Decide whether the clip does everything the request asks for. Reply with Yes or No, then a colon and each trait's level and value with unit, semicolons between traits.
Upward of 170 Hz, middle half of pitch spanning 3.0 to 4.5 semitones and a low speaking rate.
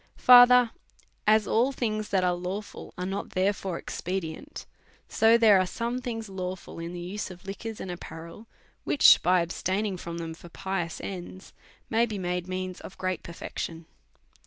No: high, 190 Hz; average, 3.6 semitones; average, 175 wpm